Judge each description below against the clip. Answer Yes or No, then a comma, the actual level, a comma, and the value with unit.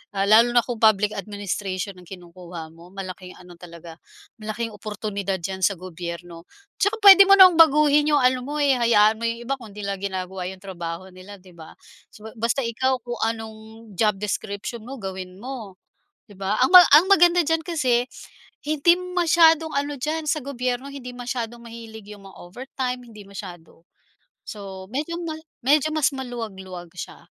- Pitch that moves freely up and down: Yes, wide, 6.2 semitones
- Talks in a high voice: Yes, high, 220 Hz